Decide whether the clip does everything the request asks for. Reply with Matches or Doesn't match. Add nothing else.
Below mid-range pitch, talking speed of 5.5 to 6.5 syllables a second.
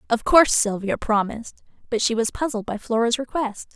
Doesn't match